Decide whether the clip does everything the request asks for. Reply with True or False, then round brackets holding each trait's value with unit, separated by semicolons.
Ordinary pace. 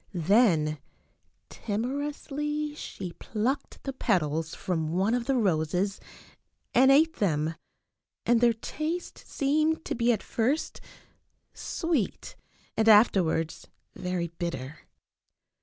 False (105 wpm)